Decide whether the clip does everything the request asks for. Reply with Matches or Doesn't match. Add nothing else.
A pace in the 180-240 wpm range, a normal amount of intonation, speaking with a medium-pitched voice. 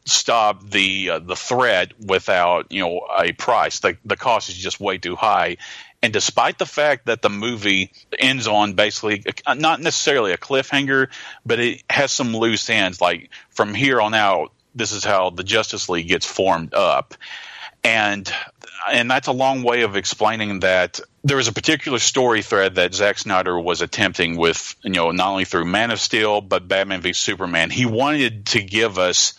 Doesn't match